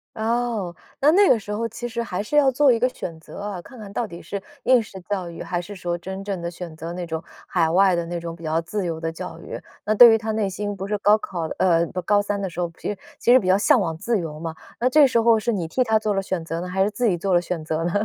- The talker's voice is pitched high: Yes, high, 195 Hz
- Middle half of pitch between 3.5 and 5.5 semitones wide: Yes, average, 4.5 semitones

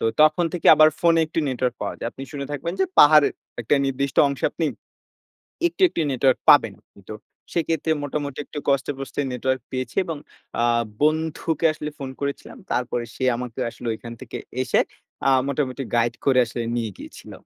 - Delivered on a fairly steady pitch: No, average, 3.3 semitones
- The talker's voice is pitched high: No, medium, 140 Hz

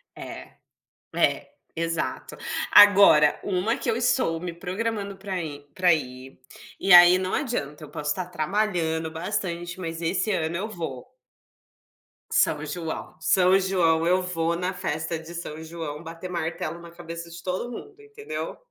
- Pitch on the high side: No, medium, 170 Hz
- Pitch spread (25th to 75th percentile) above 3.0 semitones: No, average, 2.7 semitones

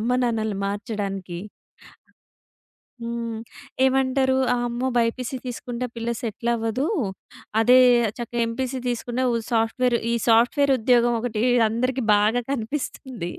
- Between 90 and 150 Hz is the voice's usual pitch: No, high, 235 Hz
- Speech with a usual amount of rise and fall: No, narrow, 2.1 semitones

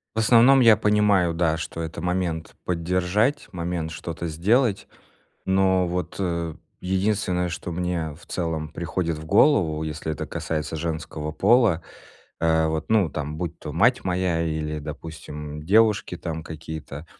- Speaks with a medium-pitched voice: No, very low, 85 Hz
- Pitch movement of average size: Yes, average, 3.2 semitones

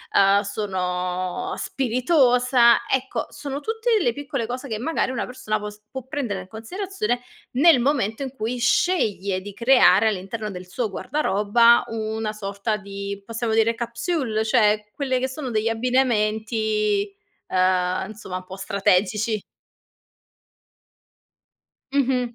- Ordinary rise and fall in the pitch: Yes, average, 4.0 semitones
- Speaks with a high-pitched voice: Yes, high, 225 Hz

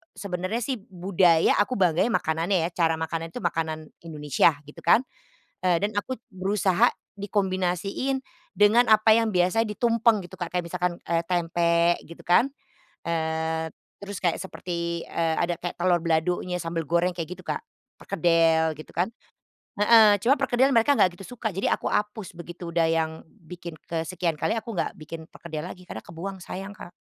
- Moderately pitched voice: Yes, medium, 175 Hz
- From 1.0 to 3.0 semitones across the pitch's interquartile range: No, average, 3.5 semitones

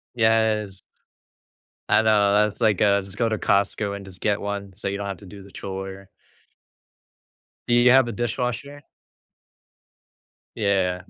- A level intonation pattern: Yes, narrow, 2.1 semitones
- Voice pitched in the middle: No, low, 100 Hz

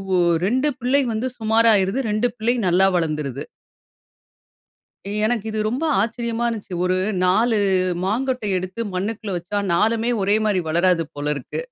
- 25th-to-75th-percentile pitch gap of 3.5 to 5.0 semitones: Yes, average, 4.2 semitones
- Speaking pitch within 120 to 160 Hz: No, high, 215 Hz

